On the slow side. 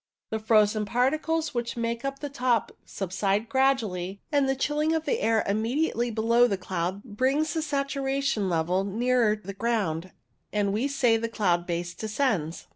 No: average, 160 wpm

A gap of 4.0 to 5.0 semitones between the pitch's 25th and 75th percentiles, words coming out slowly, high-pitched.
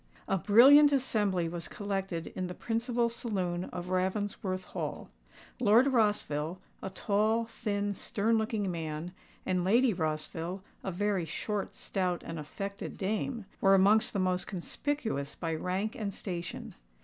No: average, 3.4 semitones; slow, 125 wpm; high, 195 Hz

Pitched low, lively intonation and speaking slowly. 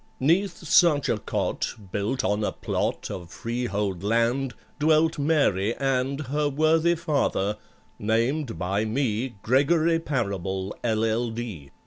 Yes: low, 125 Hz; wide, 6.1 semitones; slow, 115 wpm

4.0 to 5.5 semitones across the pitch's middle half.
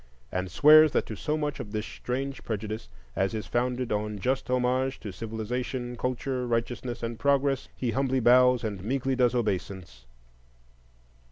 No: average, 3.3 semitones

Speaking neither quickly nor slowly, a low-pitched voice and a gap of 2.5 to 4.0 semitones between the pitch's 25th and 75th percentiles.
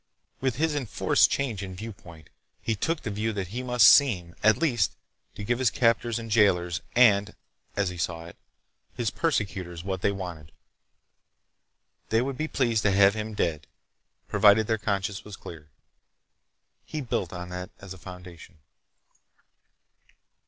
No: average, 145 wpm; low, 105 Hz; average, 4.4 semitones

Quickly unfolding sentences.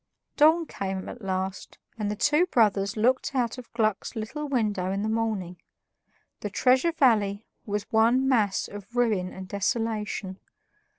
No: average, 145 wpm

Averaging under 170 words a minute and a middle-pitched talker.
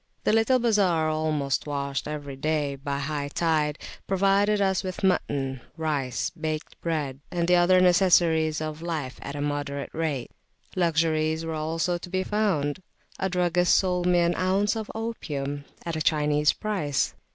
Yes: average, 150 wpm; medium, 160 Hz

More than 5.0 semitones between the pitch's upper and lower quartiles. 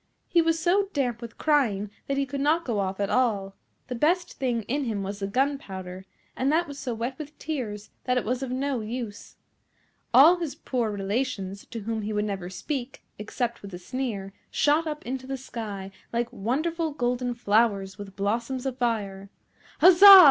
Yes: wide, 5.4 semitones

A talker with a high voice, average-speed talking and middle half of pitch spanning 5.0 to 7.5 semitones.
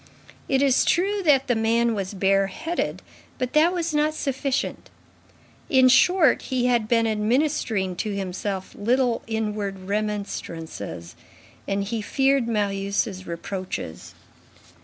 No: high, 225 Hz; slow, 115 wpm; average, 5.3 semitones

